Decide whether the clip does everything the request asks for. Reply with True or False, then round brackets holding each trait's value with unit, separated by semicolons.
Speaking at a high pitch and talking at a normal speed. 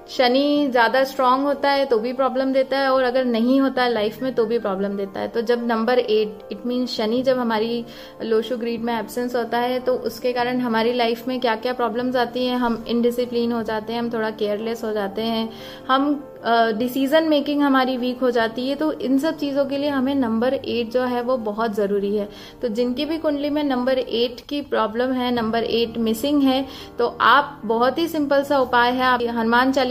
False (245 Hz; 215 wpm)